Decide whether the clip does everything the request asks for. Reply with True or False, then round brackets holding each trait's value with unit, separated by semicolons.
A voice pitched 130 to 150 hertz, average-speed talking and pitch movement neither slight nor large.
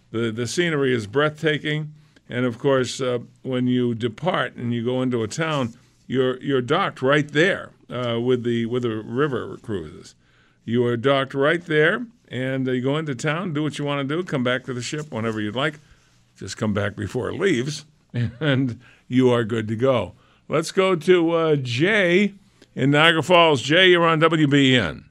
True (135 Hz; 190 wpm; 3.9 semitones)